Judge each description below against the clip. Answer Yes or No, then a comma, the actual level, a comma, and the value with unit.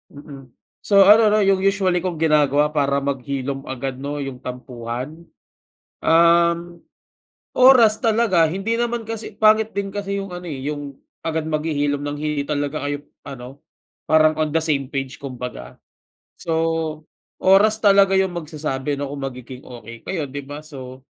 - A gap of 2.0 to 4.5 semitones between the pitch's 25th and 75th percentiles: No, average, 5.3 semitones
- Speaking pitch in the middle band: Yes, medium, 155 Hz